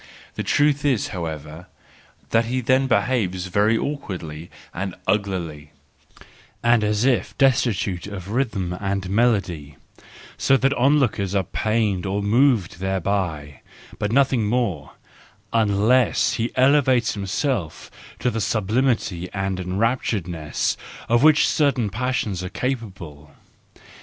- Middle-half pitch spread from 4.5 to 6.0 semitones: Yes, average, 5.2 semitones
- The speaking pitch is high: No, low, 105 Hz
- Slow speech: Yes, slow, 115 wpm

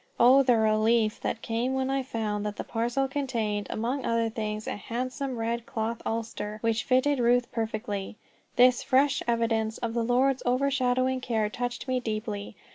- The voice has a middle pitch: No, high, 235 Hz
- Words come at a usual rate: Yes, average, 165 wpm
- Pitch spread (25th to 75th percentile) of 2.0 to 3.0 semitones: Yes, narrow, 2.6 semitones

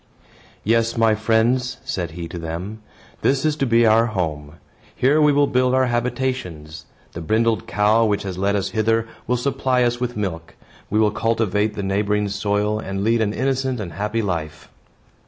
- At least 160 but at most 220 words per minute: Yes, average, 175 wpm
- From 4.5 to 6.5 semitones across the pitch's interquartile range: No, average, 3.8 semitones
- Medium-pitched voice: No, low, 110 Hz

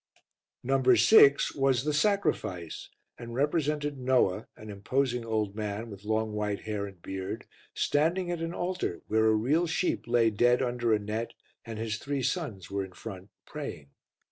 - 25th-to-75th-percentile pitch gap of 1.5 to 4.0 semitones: No, average, 5.1 semitones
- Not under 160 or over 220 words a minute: Yes, average, 165 wpm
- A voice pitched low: Yes, low, 115 Hz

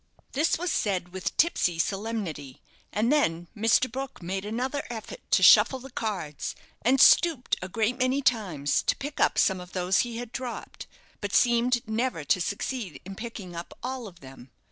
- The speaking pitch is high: Yes, high, 220 Hz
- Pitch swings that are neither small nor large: No, wide, 5.7 semitones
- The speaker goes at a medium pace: Yes, average, 175 wpm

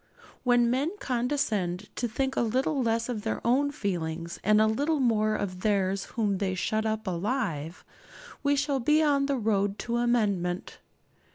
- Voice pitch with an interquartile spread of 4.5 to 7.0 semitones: Yes, average, 4.9 semitones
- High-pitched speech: Yes, high, 225 Hz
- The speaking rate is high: No, average, 165 wpm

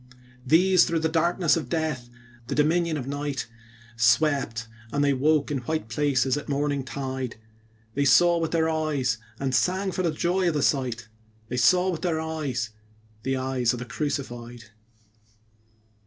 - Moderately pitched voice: Yes, medium, 145 Hz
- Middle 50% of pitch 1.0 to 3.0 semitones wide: No, average, 4.0 semitones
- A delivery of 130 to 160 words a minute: Yes, average, 155 wpm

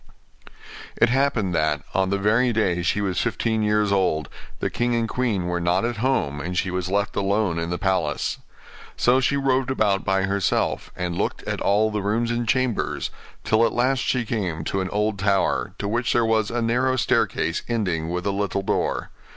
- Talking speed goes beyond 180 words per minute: Yes, average, 195 wpm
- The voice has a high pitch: No, low, 105 Hz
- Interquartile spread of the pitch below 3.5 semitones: No, average, 4.1 semitones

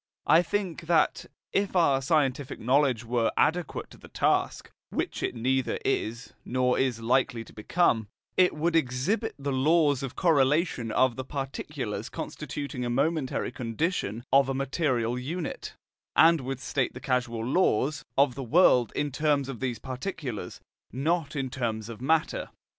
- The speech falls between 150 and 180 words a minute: Yes, average, 155 wpm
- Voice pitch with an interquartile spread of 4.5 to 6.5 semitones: No, average, 4.0 semitones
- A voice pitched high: No, low, 135 Hz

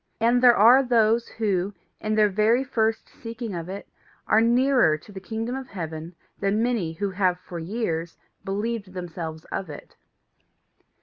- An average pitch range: Yes, average, 4.4 semitones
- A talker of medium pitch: No, high, 210 Hz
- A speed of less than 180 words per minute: Yes, average, 160 wpm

